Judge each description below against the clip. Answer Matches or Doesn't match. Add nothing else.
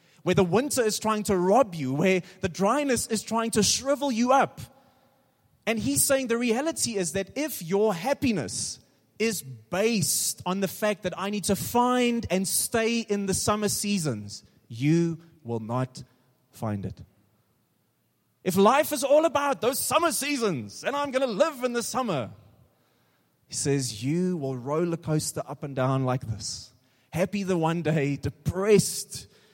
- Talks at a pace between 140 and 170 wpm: Matches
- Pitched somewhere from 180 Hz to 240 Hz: Matches